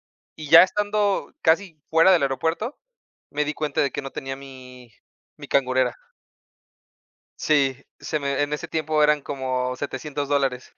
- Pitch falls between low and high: Yes, medium, 145 Hz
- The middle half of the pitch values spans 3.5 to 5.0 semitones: No, average, 2.9 semitones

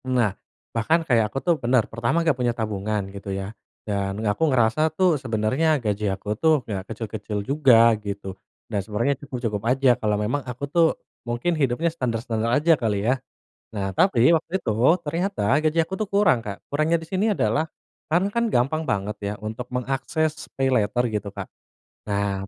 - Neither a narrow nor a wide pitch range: No, wide, 6.4 semitones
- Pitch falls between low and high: No, low, 120 Hz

